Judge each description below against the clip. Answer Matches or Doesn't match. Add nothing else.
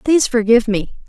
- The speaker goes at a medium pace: Matches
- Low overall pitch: Doesn't match